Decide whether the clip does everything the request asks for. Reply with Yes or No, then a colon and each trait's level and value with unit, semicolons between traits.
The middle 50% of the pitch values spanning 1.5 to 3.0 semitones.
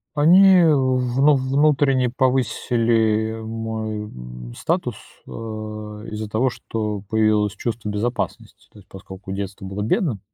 No: average, 3.5 semitones